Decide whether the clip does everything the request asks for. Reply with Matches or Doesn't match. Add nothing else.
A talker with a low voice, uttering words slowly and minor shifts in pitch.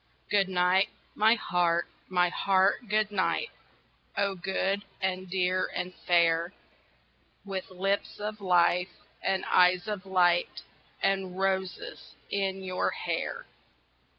Doesn't match